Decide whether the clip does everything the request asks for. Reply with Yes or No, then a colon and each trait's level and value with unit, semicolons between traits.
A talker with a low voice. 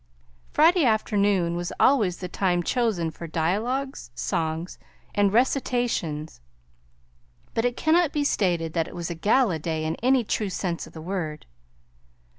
No: high, 190 Hz